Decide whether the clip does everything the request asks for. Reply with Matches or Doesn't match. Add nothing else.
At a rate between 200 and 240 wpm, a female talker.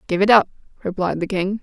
Matches